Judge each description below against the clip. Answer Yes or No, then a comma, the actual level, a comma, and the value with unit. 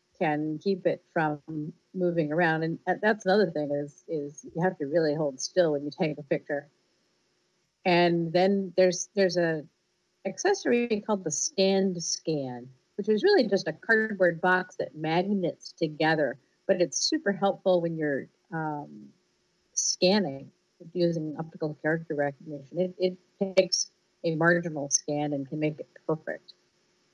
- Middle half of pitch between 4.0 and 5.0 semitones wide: No, average, 3.4 semitones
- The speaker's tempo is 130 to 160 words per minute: Yes, average, 145 wpm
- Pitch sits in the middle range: Yes, medium, 170 Hz